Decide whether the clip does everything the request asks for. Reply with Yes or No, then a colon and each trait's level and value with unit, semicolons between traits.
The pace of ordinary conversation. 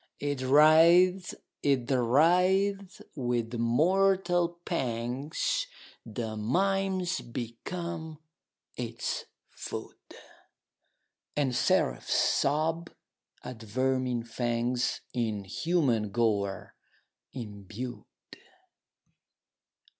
No: slow, 70 wpm